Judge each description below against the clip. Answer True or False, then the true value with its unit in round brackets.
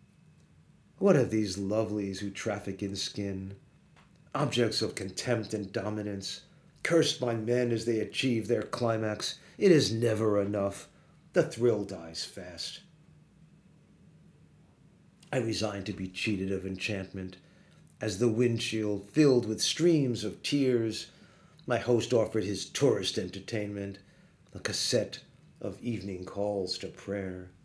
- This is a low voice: True (110 Hz)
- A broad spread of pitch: True (6.6 semitones)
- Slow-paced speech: True (125 wpm)